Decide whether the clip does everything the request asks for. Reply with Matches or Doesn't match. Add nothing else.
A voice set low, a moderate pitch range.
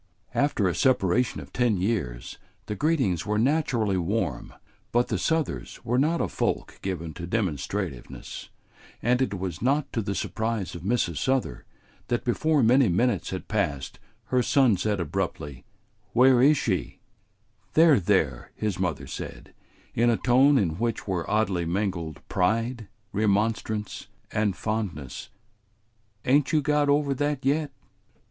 Doesn't match